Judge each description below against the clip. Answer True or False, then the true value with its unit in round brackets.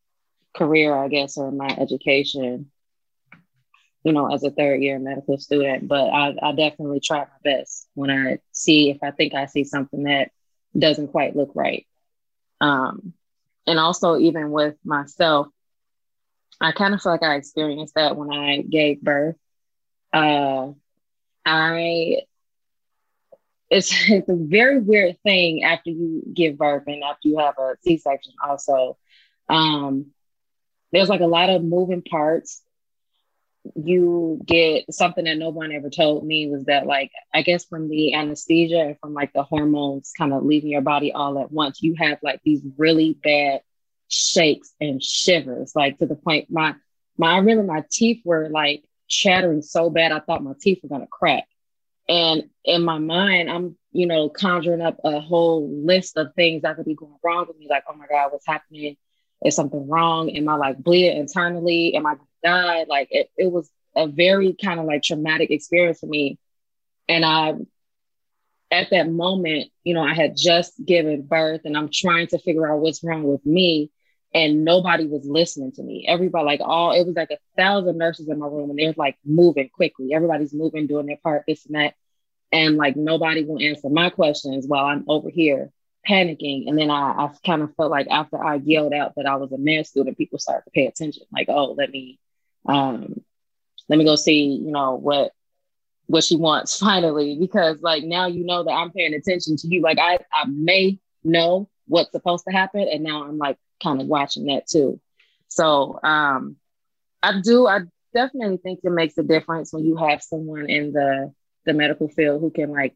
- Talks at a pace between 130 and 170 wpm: False (180 wpm)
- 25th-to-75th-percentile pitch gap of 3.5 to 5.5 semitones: False (2.7 semitones)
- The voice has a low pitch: False (155 Hz)